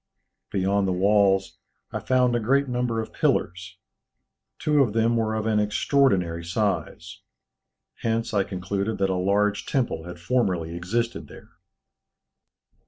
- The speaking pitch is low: Yes, low, 105 Hz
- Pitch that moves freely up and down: No, average, 3.8 semitones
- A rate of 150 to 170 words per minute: No, slow, 135 wpm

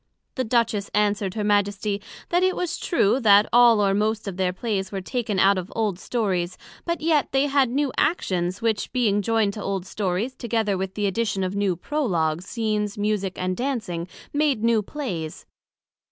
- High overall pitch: Yes, high, 210 Hz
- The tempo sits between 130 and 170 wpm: No, average, 180 wpm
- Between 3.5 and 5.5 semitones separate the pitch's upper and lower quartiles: Yes, average, 3.8 semitones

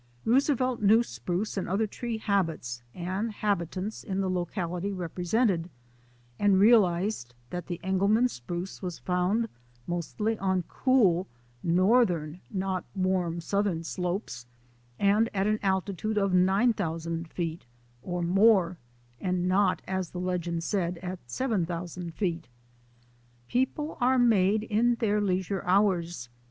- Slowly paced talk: Yes, slow, 120 wpm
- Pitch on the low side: No, high, 190 Hz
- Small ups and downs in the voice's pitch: No, average, 3.4 semitones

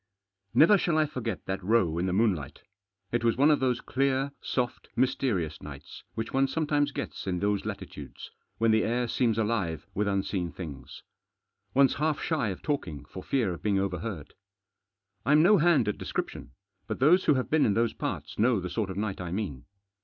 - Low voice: Yes, low, 115 Hz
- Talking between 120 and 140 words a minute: No, average, 190 wpm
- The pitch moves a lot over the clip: Yes, wide, 6.4 semitones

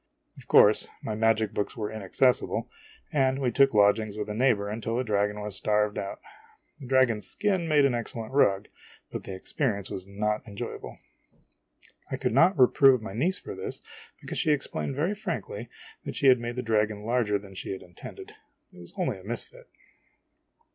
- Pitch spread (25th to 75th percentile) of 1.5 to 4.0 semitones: No, average, 4.5 semitones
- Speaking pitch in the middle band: No, low, 115 Hz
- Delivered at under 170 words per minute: No, average, 180 wpm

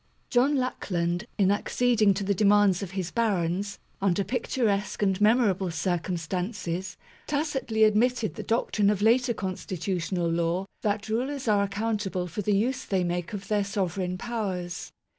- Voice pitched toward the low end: No, high, 200 Hz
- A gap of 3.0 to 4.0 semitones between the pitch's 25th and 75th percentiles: Yes, average, 3.4 semitones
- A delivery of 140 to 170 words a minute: Yes, average, 150 wpm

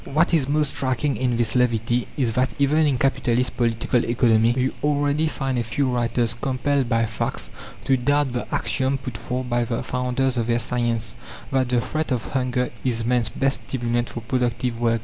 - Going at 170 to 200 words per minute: Yes, average, 190 wpm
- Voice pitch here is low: Yes, low, 125 Hz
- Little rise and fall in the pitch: Yes, narrow, 2.3 semitones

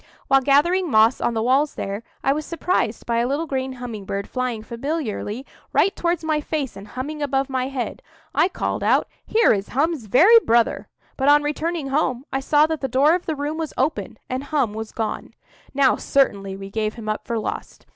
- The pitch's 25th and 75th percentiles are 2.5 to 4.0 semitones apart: No, average, 4.8 semitones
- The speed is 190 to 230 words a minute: Yes, fast, 205 wpm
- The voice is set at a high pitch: Yes, very high, 270 Hz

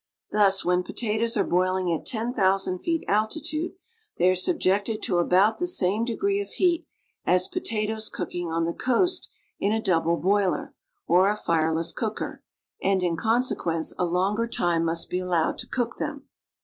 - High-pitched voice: Yes, high, 195 Hz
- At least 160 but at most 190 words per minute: Yes, average, 170 wpm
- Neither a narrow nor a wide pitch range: Yes, average, 4.2 semitones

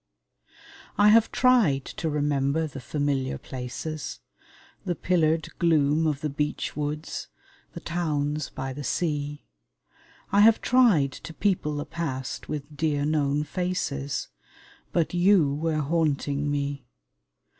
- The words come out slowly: Yes, slow, 120 wpm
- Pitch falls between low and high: Yes, medium, 150 Hz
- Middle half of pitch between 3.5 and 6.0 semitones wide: No, average, 2.7 semitones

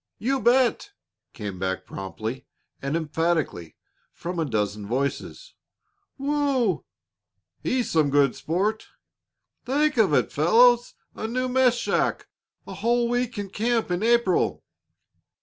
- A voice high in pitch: Yes, high, 205 Hz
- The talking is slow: Yes, slow, 120 wpm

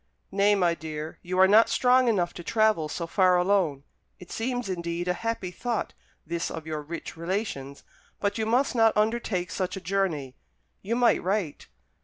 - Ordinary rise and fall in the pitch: Yes, average, 4.4 semitones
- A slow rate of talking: No, average, 175 wpm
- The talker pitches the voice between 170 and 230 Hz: Yes, medium, 185 Hz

